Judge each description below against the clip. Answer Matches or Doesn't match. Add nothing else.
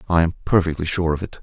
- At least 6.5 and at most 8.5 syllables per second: Matches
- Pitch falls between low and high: Doesn't match